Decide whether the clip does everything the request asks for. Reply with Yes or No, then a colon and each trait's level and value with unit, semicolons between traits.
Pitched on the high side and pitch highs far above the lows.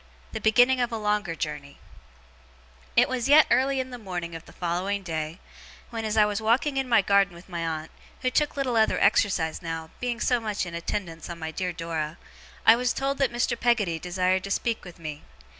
Yes: high, 200 Hz; wide, 6.2 semitones